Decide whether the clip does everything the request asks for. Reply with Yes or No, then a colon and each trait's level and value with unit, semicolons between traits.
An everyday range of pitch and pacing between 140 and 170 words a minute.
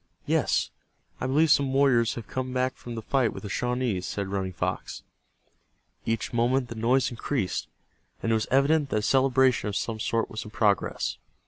No: average, 3.3 semitones; average, 185 wpm